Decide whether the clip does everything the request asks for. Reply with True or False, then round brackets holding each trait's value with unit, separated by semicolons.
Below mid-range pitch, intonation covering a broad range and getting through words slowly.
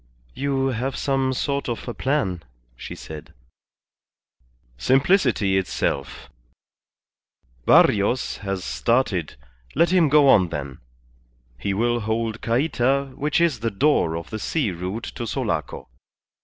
True (120 Hz; 6.0 semitones; 120 wpm)